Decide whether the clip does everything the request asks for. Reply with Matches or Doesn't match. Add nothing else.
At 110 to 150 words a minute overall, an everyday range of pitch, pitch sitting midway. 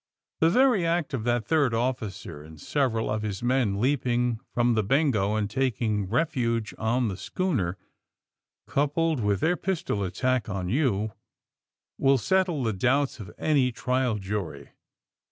Doesn't match